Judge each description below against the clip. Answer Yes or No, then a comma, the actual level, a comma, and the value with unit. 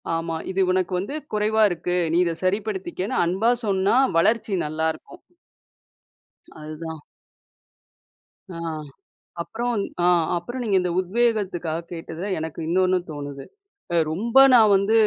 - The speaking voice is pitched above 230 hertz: No, medium, 185 Hz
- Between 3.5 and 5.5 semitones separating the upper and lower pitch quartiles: Yes, average, 4.3 semitones